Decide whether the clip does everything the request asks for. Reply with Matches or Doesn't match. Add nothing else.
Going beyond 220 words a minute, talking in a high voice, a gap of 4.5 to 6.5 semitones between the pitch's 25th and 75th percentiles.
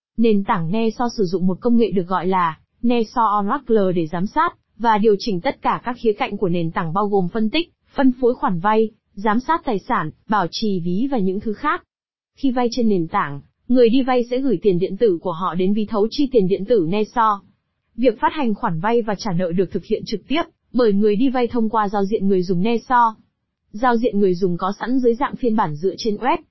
Doesn't match